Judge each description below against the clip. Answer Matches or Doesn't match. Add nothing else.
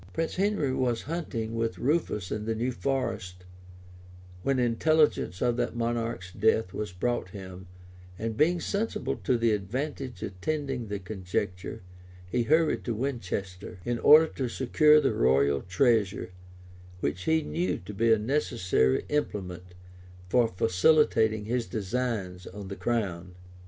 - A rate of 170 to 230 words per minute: Doesn't match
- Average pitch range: Doesn't match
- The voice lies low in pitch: Matches